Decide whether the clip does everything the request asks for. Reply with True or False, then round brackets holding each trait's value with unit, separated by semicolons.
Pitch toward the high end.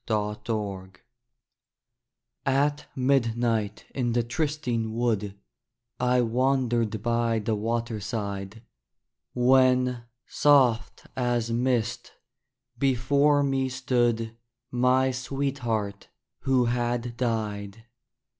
False (120 Hz)